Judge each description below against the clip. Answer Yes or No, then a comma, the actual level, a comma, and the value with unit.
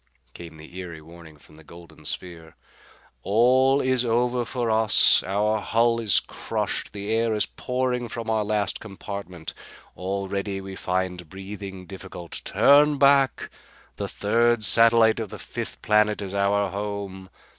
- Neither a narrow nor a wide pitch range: Yes, average, 3.7 semitones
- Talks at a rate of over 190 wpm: No, average, 145 wpm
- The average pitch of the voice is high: No, low, 100 Hz